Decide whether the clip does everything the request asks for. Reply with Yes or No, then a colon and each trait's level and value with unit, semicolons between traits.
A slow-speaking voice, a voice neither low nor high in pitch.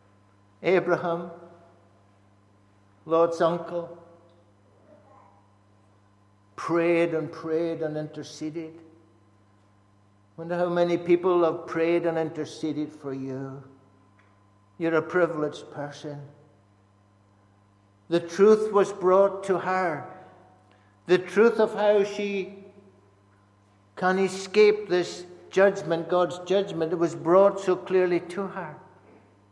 Yes: slow, 95 wpm; medium, 160 Hz